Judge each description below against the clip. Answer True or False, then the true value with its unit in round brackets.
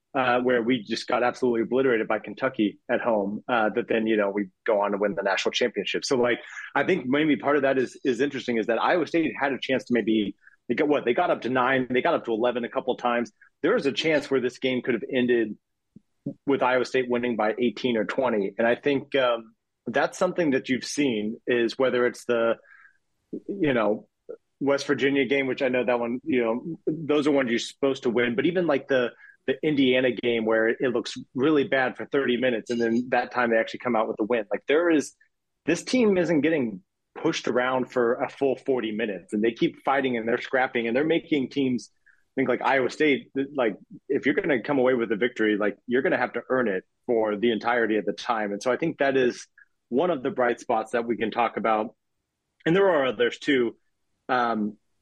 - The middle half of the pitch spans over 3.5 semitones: False (2.9 semitones)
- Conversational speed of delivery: False (230 wpm)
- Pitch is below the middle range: True (125 Hz)